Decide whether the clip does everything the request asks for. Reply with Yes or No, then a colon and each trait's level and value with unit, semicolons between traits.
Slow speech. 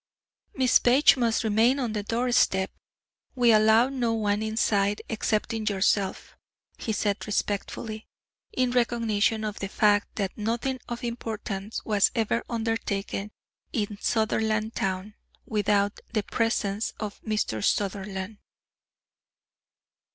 Yes: slow, 110 wpm